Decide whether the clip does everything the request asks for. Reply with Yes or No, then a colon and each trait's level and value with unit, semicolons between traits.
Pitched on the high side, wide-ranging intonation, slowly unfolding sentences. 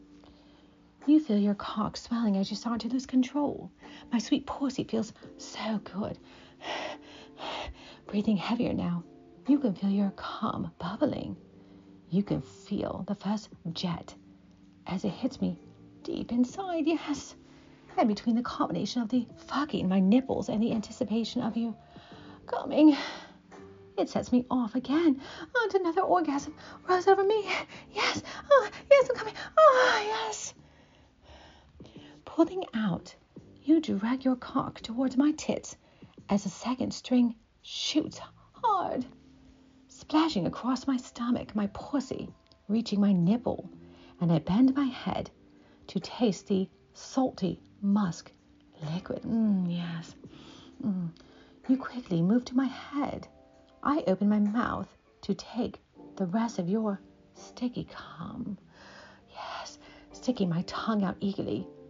Yes: high, 230 Hz; wide, 5.8 semitones; slow, 130 wpm